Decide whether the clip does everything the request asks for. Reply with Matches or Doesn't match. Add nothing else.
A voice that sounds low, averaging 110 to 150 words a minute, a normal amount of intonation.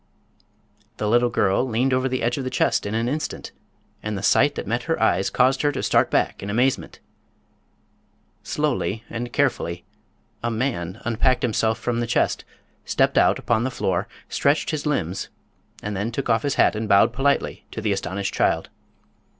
Doesn't match